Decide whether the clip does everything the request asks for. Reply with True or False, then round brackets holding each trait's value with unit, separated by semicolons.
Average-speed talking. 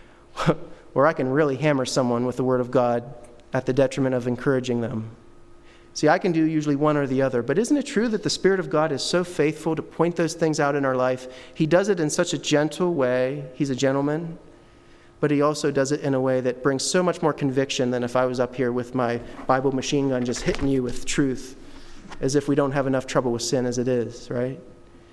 False (240 wpm)